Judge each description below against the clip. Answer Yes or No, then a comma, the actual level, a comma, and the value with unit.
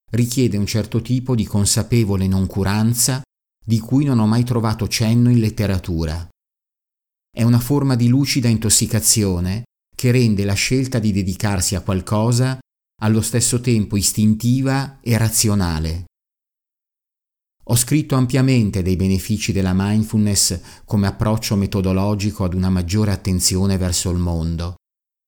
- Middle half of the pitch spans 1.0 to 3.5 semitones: No, average, 3.9 semitones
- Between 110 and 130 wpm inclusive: Yes, average, 125 wpm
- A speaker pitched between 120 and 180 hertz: No, low, 105 Hz